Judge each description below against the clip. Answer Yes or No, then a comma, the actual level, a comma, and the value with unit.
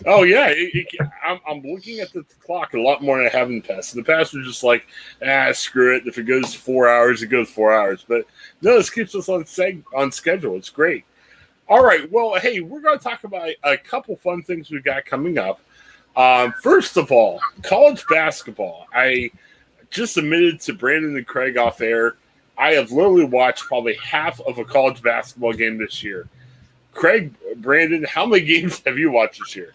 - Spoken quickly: Yes, fast, 210 wpm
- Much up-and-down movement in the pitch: Yes, wide, 6.3 semitones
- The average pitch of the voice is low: No, medium, 145 Hz